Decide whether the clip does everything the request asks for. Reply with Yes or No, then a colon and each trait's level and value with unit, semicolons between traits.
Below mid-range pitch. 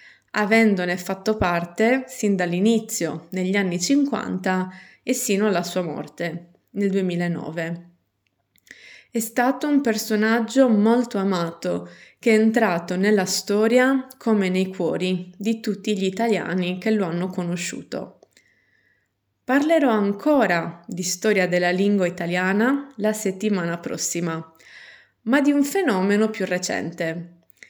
No: high, 195 Hz